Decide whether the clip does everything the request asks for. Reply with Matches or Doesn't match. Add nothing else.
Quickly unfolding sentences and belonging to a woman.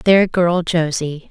Doesn't match